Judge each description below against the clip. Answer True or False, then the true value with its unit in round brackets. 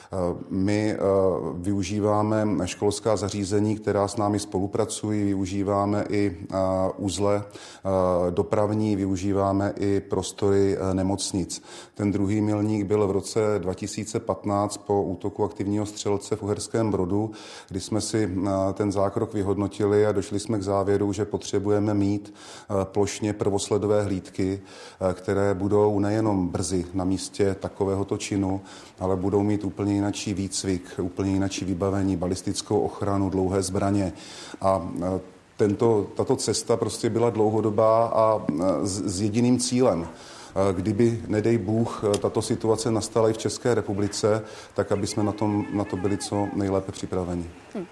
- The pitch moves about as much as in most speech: False (1.4 semitones)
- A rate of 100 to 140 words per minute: True (125 wpm)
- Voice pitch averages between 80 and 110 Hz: True (100 Hz)